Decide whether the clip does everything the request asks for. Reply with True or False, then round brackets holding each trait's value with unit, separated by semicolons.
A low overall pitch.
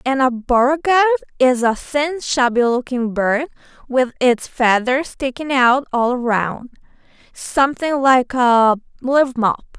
False (260 Hz)